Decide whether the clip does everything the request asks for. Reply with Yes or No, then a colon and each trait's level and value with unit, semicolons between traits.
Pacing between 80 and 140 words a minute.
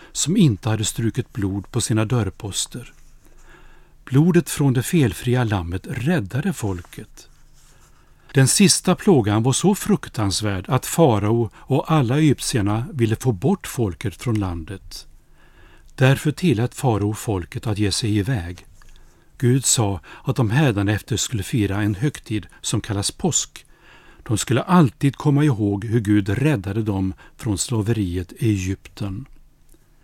Yes: average, 130 wpm